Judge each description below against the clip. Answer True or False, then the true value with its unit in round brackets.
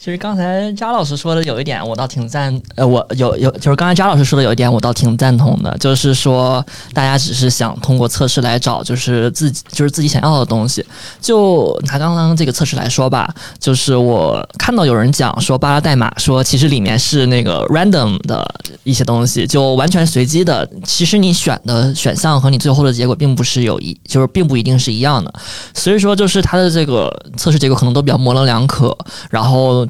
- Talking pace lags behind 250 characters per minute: False (340 characters per minute)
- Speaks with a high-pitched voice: False (135 Hz)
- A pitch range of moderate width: True (3.7 semitones)